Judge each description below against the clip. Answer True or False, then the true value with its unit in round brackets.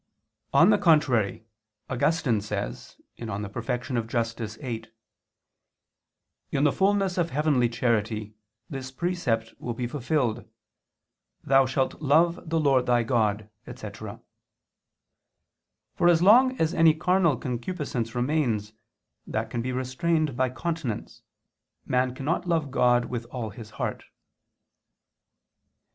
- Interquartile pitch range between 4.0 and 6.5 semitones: True (5.5 semitones)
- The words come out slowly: True (115 wpm)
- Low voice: True (130 Hz)